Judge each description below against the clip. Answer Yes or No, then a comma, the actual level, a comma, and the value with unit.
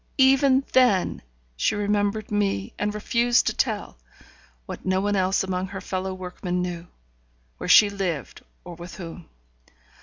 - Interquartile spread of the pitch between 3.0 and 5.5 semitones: No, narrow, 2.5 semitones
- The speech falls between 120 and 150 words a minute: Yes, average, 145 wpm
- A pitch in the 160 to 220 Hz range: Yes, high, 190 Hz